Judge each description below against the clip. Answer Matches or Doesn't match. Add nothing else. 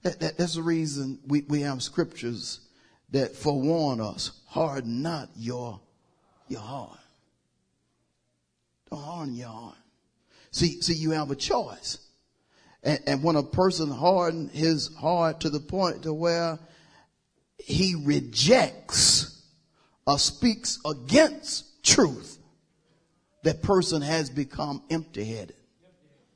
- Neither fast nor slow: Doesn't match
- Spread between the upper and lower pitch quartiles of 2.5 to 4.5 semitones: Matches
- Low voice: Doesn't match